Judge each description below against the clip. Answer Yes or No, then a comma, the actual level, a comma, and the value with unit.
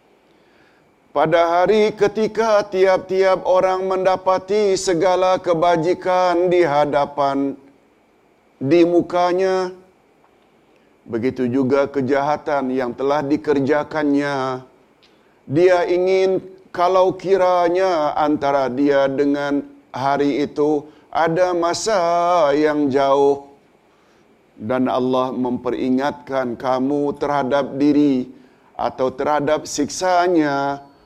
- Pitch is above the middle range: No, medium, 150 Hz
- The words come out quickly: No, average, 75 wpm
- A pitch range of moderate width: Yes, average, 4.6 semitones